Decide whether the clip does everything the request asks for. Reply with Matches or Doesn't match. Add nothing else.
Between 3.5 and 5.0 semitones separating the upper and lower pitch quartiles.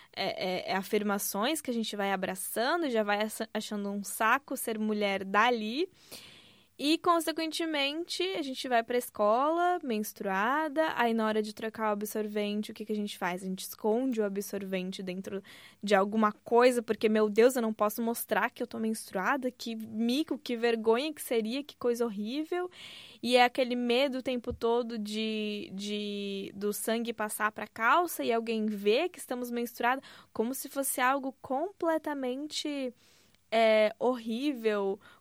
Matches